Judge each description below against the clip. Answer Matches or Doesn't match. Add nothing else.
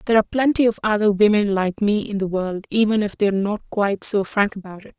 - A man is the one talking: Doesn't match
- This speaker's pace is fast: Matches